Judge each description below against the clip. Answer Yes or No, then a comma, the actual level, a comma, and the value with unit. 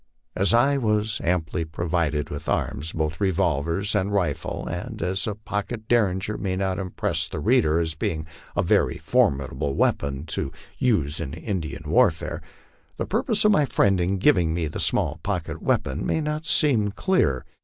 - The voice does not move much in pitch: No, average, 5.1 semitones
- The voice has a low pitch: Yes, very low, 90 Hz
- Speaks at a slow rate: No, average, 165 wpm